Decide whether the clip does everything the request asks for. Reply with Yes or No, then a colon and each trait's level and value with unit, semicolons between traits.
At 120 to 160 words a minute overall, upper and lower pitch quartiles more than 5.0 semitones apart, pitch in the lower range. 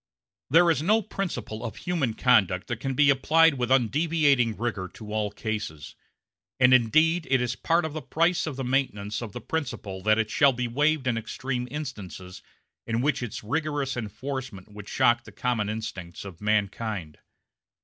No: average, 170 wpm; wide, 5.4 semitones; low, 125 Hz